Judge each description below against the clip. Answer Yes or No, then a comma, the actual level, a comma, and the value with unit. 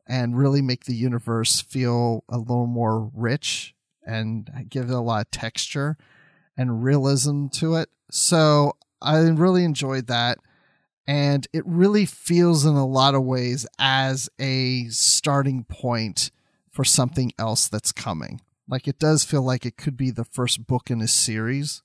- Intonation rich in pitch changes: No, average, 3.2 semitones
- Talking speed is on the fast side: No, average, 160 wpm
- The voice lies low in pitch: Yes, low, 130 Hz